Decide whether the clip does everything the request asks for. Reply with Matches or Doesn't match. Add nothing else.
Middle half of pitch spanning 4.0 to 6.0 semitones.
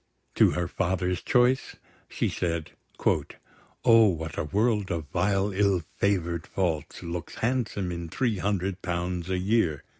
Doesn't match